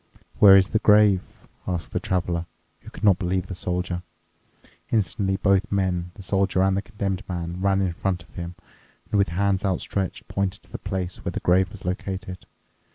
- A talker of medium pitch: No, very low, 95 Hz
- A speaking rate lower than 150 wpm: No, average, 185 wpm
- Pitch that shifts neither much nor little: No, narrow, 1.6 semitones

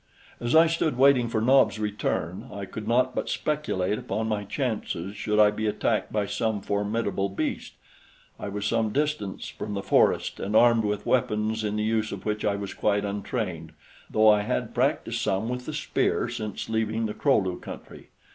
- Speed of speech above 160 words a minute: Yes, average, 185 wpm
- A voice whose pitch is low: Yes, low, 105 Hz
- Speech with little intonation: Yes, narrow, 2.3 semitones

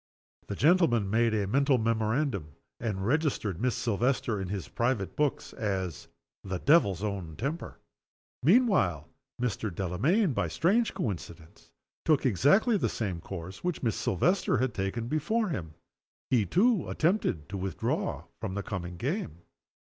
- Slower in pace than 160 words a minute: Yes, average, 140 wpm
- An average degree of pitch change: No, wide, 7.8 semitones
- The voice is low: Yes, low, 115 Hz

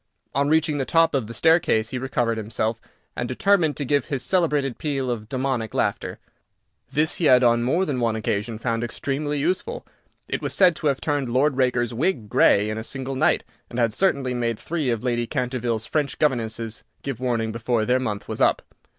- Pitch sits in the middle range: No, low, 125 Hz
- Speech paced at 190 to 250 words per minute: Yes, average, 195 wpm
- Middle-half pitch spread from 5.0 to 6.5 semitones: No, average, 3.9 semitones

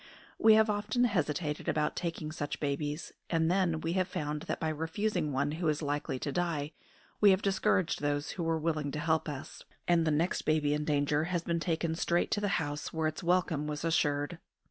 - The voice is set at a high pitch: No, medium, 160 Hz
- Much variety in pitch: No, average, 2.8 semitones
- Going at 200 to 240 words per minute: Yes, fast, 205 wpm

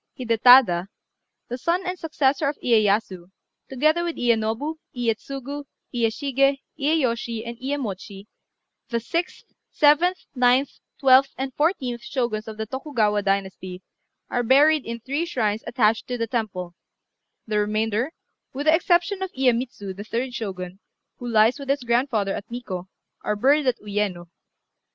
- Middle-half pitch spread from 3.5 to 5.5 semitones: Yes, average, 4.6 semitones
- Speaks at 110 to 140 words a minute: Yes, slow, 135 wpm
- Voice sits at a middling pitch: No, high, 245 Hz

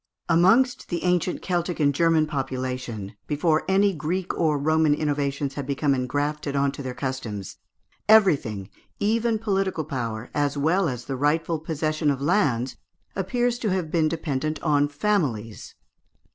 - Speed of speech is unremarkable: Yes, average, 145 wpm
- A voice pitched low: No, medium, 150 Hz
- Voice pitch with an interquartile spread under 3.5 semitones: No, average, 4.3 semitones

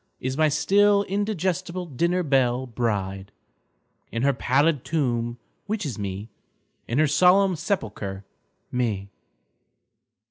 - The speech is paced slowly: Yes, slow, 110 wpm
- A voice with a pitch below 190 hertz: Yes, medium, 140 Hz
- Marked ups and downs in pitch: Yes, wide, 7.6 semitones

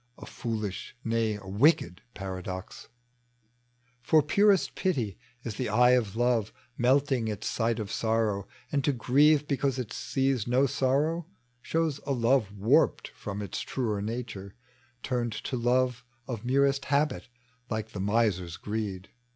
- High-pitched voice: No, low, 120 Hz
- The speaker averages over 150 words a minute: No, average, 140 wpm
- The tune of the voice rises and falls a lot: No, average, 4.5 semitones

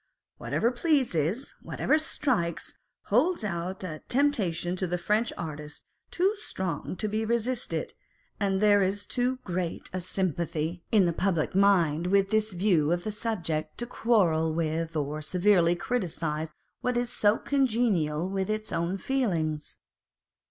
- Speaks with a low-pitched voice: No, high, 190 Hz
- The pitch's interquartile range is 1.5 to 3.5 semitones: No, average, 5.0 semitones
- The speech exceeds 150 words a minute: No, average, 145 wpm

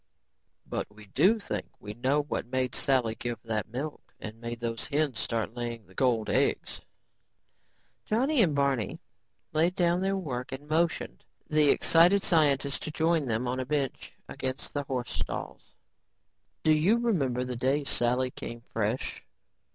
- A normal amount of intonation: Yes, average, 4.7 semitones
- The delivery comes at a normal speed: Yes, average, 155 wpm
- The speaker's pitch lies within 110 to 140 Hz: Yes, low, 135 Hz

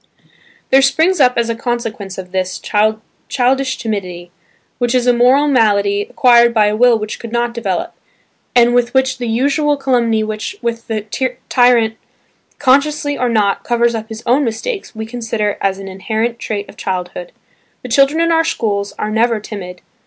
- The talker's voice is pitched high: Yes, high, 235 Hz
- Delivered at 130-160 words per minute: No, average, 170 wpm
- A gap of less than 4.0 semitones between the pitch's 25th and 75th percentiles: Yes, average, 2.9 semitones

